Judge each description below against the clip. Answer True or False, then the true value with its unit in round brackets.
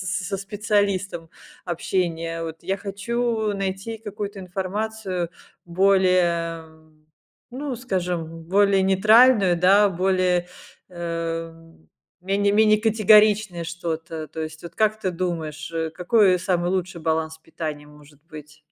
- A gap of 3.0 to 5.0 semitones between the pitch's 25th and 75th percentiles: True (3.5 semitones)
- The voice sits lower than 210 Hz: True (185 Hz)